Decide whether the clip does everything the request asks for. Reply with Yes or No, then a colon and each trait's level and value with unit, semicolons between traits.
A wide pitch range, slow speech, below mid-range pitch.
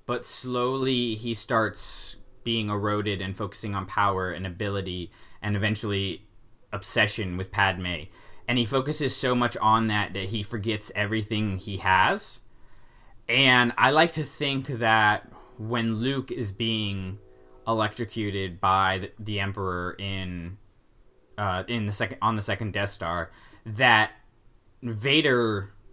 No: average, 3.1 semitones; slow, 130 wpm; low, 105 Hz